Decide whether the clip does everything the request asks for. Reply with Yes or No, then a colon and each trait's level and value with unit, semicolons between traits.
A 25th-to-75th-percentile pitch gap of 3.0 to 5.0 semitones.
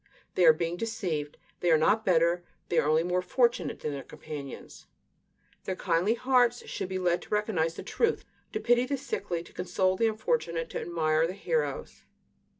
No: wide, 5.5 semitones